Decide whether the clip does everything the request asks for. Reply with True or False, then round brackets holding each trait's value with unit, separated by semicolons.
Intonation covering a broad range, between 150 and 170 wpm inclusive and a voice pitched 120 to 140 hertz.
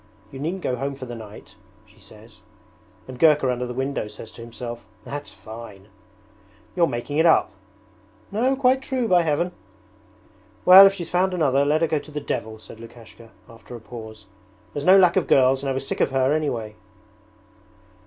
False (6.1 semitones; 185 wpm; 135 Hz)